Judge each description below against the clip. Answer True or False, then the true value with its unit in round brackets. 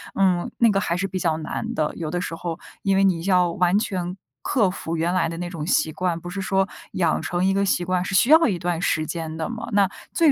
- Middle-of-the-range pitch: True (180 Hz)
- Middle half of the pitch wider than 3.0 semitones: False (2.6 semitones)